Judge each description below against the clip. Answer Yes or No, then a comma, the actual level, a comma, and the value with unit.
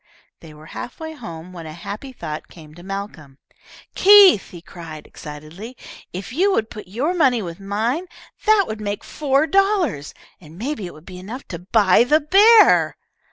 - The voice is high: Yes, high, 205 Hz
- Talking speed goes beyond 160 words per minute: Yes, average, 175 wpm